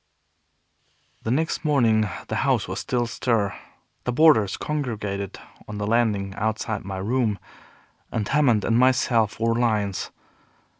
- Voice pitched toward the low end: Yes, low, 115 Hz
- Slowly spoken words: Yes, slow, 130 wpm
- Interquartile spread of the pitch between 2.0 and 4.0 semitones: Yes, average, 3.2 semitones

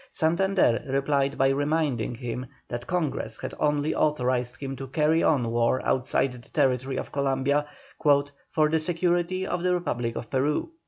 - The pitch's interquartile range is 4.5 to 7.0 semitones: No, average, 3.8 semitones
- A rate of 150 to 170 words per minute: Yes, average, 155 wpm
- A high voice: No, medium, 140 Hz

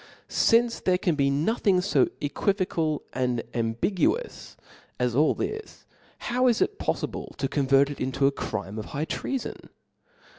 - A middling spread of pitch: No, wide, 8.0 semitones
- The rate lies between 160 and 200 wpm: No, average, 150 wpm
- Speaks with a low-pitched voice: No, medium, 150 Hz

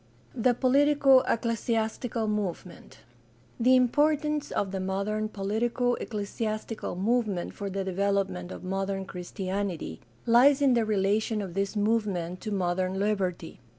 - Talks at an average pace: No, slow, 120 wpm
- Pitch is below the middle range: No, high, 210 Hz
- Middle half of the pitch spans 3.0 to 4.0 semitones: Yes, average, 3.6 semitones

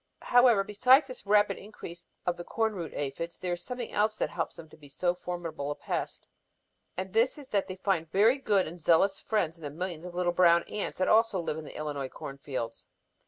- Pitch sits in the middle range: Yes, medium, 180 Hz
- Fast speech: Yes, fast, 220 wpm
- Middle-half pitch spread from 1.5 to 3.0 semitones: No, average, 4.3 semitones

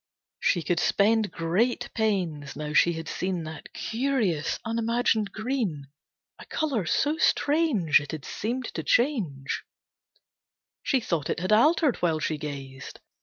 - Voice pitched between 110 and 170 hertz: No, high, 195 Hz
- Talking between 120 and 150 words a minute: Yes, slow, 135 wpm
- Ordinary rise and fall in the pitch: No, wide, 7.3 semitones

